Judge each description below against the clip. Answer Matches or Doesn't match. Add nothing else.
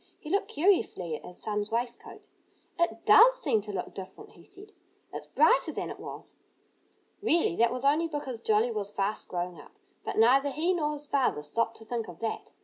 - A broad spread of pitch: Matches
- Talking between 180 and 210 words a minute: Matches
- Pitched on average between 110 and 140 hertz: Doesn't match